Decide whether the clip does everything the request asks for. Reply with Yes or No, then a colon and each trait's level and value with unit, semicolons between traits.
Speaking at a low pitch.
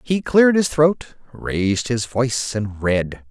Yes: low, 125 Hz